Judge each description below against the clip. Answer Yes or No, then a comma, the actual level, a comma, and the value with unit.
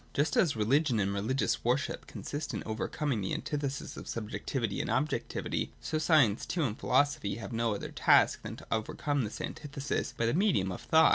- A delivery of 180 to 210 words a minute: Yes, average, 190 wpm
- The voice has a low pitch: Yes, low, 130 Hz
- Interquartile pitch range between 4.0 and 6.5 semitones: Yes, average, 5.1 semitones